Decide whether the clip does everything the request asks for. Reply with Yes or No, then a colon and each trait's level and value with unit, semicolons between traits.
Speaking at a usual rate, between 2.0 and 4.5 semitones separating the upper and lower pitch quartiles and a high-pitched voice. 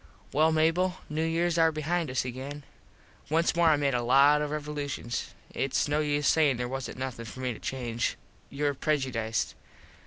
No: average, 175 wpm; average, 3.3 semitones; medium, 145 Hz